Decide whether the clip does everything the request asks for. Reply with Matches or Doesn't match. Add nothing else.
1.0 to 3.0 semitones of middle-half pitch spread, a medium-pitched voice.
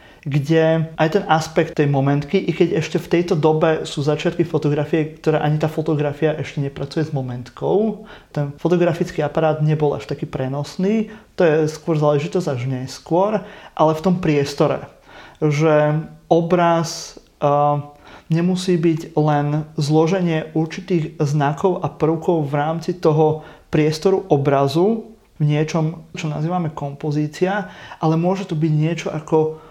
Matches